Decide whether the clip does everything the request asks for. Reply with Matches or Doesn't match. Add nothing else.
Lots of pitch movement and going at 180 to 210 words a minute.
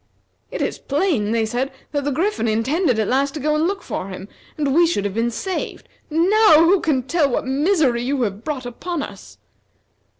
Matches